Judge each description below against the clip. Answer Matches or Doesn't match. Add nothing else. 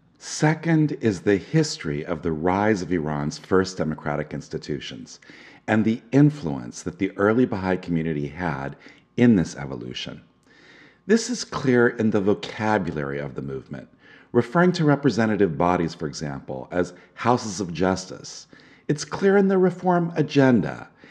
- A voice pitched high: Doesn't match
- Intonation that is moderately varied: Doesn't match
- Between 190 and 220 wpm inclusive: Doesn't match